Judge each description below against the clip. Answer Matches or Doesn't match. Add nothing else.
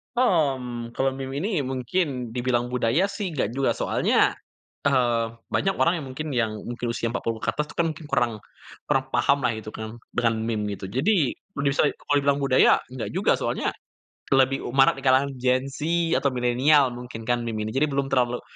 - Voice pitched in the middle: Doesn't match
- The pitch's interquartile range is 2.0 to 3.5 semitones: Matches